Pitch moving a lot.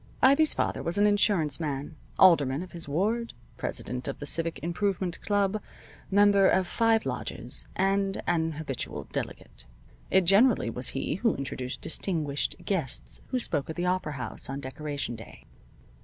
Yes: wide, 5.8 semitones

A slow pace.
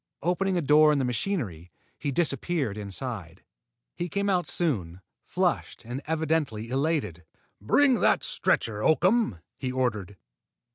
Yes: slow, 130 wpm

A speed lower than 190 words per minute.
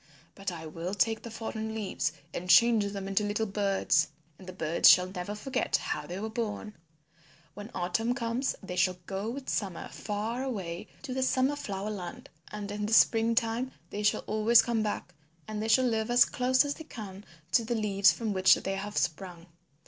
No: average, 195 wpm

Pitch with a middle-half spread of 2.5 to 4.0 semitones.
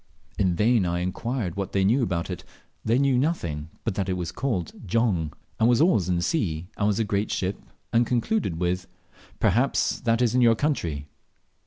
No: wide, 5.5 semitones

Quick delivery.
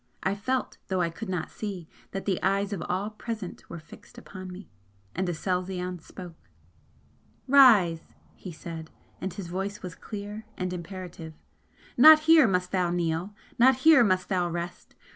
No: average, 160 wpm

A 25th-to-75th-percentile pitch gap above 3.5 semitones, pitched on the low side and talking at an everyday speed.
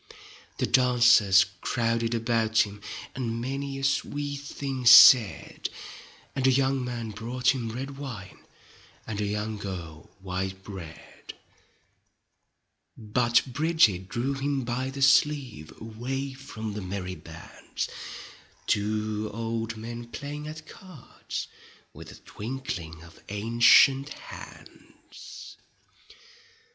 No: average, 4.4 semitones; low, 115 Hz; slow, 110 wpm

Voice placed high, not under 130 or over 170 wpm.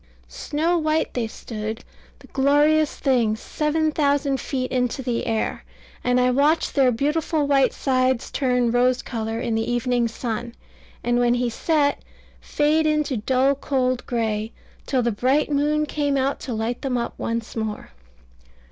Yes: very high, 255 Hz; average, 155 wpm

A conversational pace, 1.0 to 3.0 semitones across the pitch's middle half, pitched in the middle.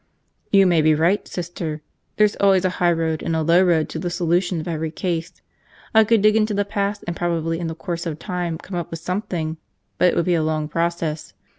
No: fast, 230 wpm; narrow, 2.4 semitones; medium, 170 Hz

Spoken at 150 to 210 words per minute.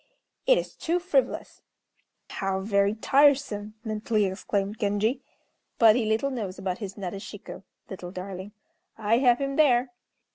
No: slow, 135 wpm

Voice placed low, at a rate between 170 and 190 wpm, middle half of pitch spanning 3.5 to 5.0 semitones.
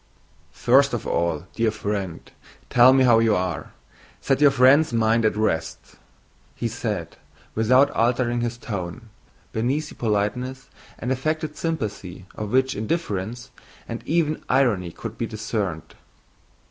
No: low, 115 Hz; slow, 135 wpm; average, 4.0 semitones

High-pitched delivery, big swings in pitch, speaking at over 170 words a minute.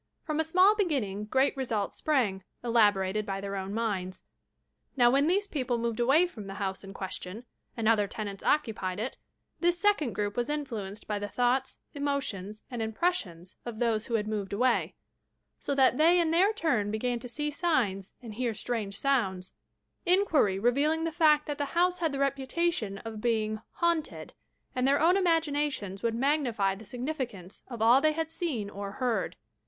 Yes: high, 240 Hz; wide, 6.5 semitones; average, 180 wpm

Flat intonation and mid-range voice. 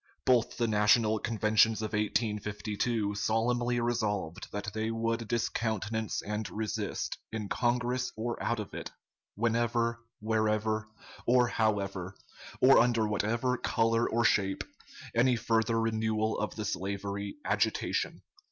No: narrow, 1.8 semitones; low, 110 Hz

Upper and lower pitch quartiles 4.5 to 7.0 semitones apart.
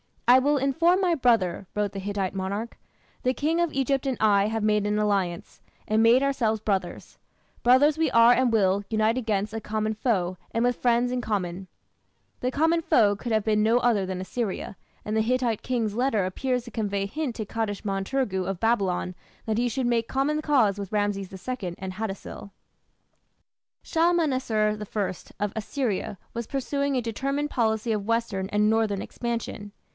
No: average, 3.8 semitones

